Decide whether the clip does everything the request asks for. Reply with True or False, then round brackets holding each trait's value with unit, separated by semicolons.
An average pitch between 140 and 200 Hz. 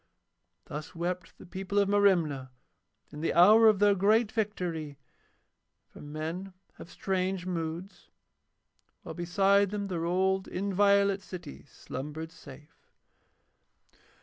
True (185 Hz)